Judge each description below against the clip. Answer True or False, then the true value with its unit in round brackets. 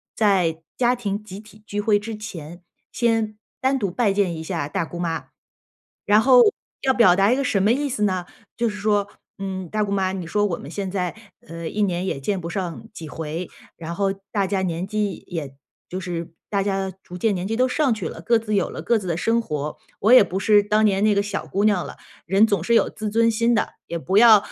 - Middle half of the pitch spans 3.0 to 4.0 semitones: True (3.4 semitones)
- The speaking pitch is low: False (200 Hz)